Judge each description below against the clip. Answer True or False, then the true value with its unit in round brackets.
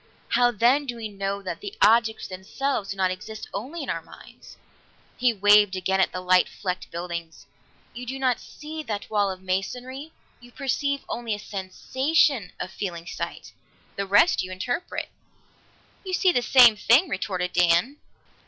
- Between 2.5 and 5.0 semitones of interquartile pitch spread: False (5.5 semitones)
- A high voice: True (215 Hz)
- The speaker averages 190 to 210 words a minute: False (170 wpm)